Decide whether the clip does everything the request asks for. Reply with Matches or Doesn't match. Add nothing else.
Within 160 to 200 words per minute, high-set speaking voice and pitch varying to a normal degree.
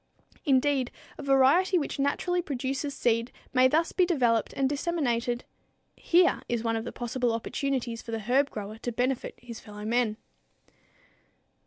Doesn't match